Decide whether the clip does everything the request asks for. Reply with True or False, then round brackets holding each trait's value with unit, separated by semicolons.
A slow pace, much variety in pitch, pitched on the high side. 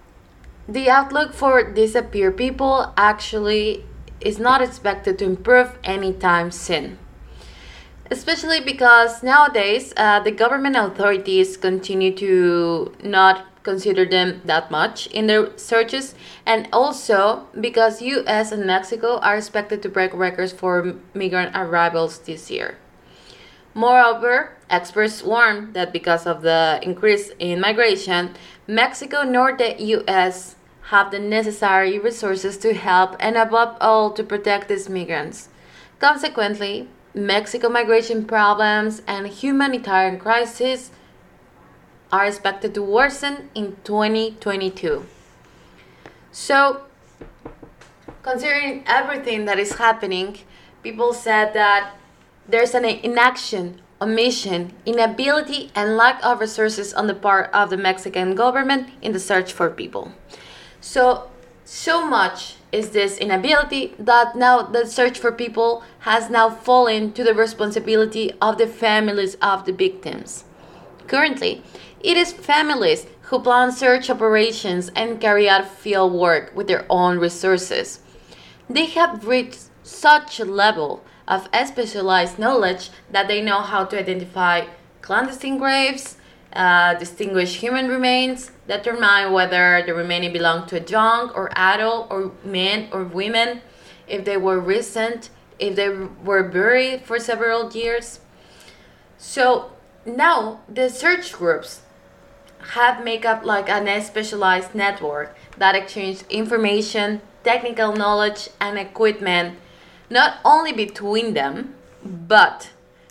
False (120 wpm; 4.0 semitones; 215 Hz)